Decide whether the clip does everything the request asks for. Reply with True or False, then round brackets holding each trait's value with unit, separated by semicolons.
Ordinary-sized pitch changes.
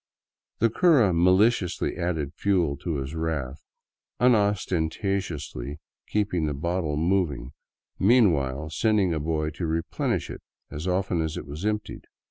True (4.3 semitones)